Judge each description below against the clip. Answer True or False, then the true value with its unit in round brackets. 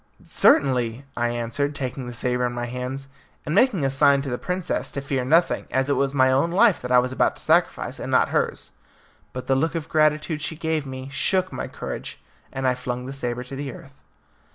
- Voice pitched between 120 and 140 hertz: True (135 Hz)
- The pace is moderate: False (220 wpm)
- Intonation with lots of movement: False (3.2 semitones)